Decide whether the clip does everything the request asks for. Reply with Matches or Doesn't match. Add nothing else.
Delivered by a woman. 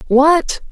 Doesn't match